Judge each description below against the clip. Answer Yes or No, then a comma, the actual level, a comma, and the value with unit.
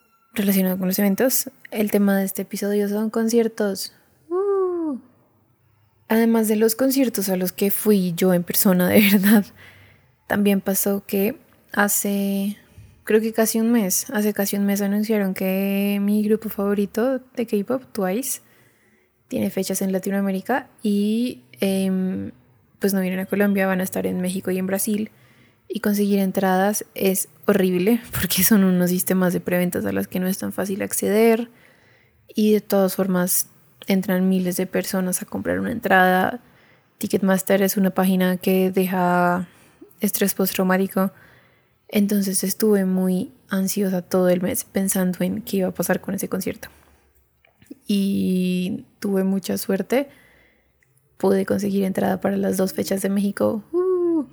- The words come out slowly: No, average, 145 wpm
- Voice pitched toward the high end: Yes, high, 195 Hz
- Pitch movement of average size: No, narrow, 2.2 semitones